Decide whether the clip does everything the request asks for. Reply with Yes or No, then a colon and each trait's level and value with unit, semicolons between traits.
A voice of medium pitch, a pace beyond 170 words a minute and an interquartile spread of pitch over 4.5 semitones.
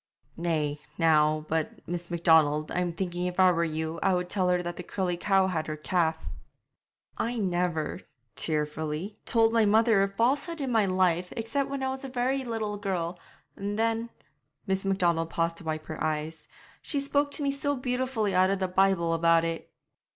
Yes: medium, 180 Hz; average, 185 wpm; average, 5.3 semitones